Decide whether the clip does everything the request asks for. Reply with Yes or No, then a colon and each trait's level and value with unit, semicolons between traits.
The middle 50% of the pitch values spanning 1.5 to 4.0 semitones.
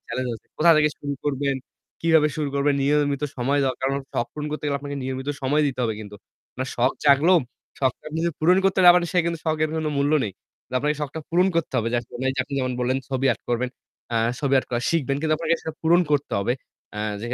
Yes: average, 3.0 semitones